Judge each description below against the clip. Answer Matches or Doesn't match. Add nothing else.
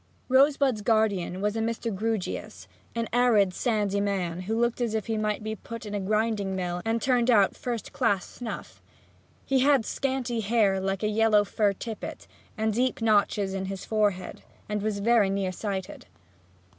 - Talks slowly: Doesn't match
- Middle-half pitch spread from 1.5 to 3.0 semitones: Matches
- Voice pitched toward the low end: Doesn't match